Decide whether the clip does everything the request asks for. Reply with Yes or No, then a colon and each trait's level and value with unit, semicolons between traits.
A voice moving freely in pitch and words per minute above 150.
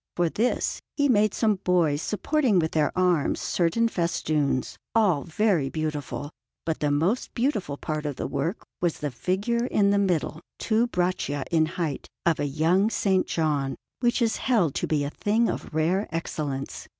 Yes: wide, 5.7 semitones; average, 170 wpm